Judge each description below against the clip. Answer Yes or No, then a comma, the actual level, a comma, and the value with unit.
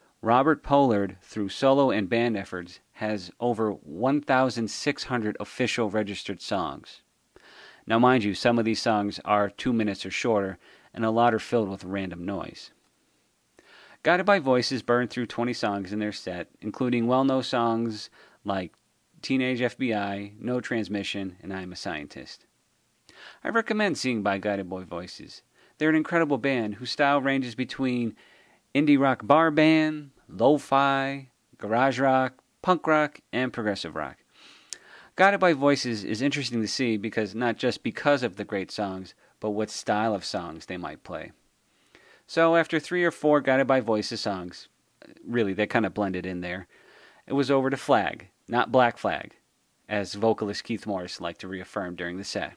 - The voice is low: Yes, low, 115 Hz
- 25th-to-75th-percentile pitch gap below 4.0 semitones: No, average, 4.8 semitones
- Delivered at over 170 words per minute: No, average, 160 wpm